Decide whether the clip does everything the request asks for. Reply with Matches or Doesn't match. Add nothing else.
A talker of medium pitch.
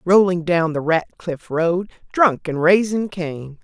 Matches